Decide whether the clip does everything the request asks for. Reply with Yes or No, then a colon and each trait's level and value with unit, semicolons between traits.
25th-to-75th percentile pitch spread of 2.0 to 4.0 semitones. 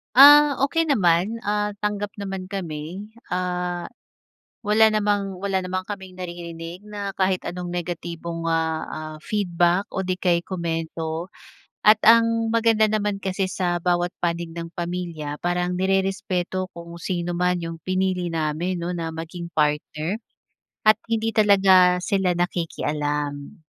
Yes: average, 2.9 semitones